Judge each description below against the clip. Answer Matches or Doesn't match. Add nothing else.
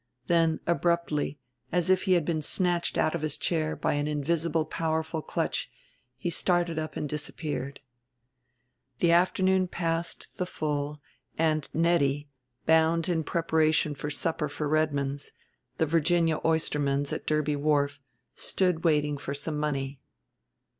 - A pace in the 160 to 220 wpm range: Doesn't match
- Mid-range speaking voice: Matches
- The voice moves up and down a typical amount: Doesn't match